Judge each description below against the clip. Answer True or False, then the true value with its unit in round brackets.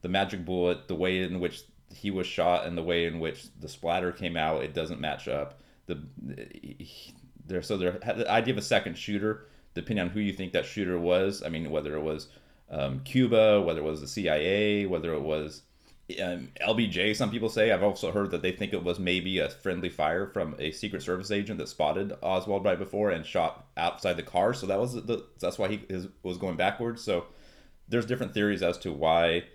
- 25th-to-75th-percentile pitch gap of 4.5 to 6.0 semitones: False (3.8 semitones)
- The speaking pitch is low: True (90 Hz)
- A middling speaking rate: False (210 wpm)